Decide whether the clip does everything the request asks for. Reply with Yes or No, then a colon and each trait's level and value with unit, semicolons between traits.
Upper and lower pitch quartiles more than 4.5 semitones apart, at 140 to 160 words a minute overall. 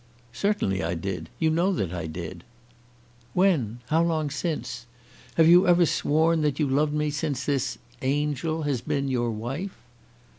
Yes: average, 5.2 semitones; average, 155 wpm